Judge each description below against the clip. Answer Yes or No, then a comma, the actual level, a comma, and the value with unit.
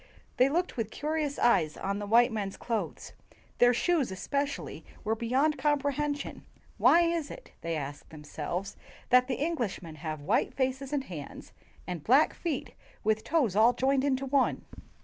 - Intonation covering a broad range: Yes, wide, 6.3 semitones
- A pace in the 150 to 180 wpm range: Yes, average, 160 wpm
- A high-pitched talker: Yes, very high, 250 Hz